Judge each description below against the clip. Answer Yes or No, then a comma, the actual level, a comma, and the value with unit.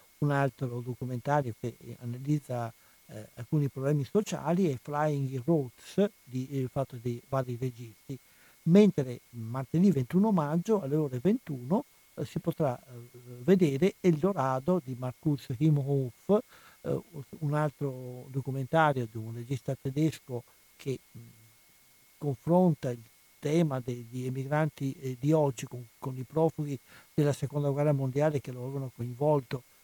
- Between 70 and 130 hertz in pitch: No, medium, 140 Hz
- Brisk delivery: No, average, 130 wpm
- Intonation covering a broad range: No, average, 3.5 semitones